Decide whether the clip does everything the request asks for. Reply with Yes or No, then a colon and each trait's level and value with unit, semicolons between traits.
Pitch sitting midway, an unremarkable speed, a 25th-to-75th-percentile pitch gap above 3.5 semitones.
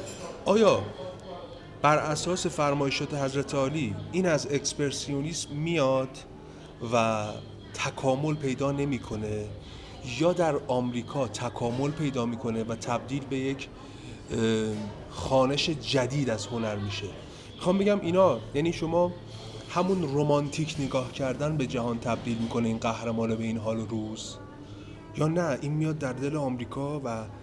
No: low, 130 Hz; average, 125 wpm; average, 4.4 semitones